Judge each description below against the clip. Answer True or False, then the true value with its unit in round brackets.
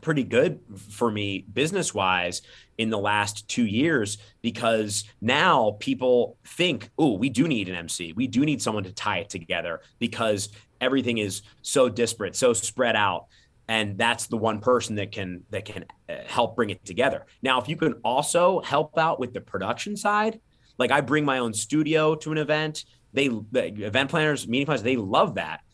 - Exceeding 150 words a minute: True (180 wpm)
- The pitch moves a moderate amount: False (6.1 semitones)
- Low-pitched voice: True (120 Hz)